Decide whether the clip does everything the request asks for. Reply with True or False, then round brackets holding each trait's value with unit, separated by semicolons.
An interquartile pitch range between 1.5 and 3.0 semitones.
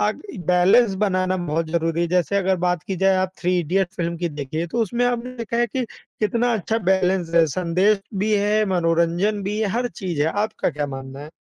False (3.9 semitones)